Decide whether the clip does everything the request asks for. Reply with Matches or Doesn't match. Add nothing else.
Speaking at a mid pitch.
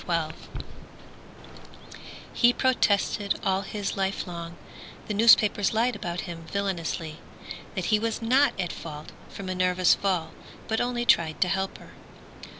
Doesn't match